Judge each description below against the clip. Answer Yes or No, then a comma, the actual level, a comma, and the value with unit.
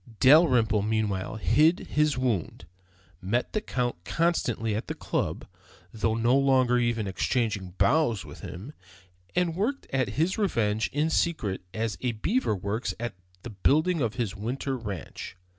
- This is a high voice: No, low, 120 Hz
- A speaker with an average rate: Yes, average, 145 wpm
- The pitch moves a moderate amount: No, wide, 5.8 semitones